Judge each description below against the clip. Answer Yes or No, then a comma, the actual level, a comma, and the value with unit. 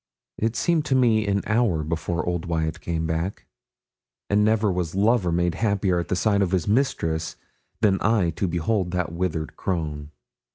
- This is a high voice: No, very low, 90 Hz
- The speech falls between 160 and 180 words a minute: Yes, average, 165 wpm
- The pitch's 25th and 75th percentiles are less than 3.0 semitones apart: No, average, 4.3 semitones